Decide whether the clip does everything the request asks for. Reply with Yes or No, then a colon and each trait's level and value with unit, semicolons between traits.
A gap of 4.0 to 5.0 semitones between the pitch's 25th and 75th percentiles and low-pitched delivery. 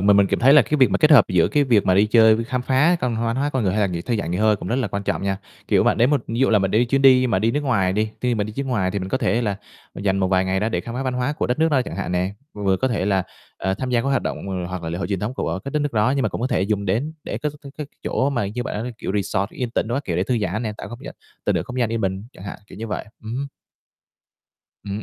Yes: average, 4.6 semitones; low, 110 Hz